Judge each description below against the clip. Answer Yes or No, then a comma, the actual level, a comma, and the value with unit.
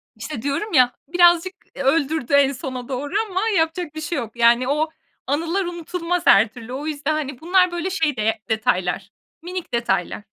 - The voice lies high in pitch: Yes, very high, 290 Hz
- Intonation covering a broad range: Yes, wide, 5.7 semitones